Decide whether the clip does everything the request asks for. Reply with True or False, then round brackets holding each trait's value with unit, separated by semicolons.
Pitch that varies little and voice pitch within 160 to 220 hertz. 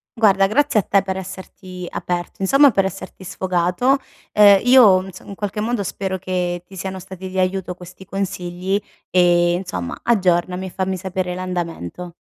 True (1.6 semitones; 190 Hz)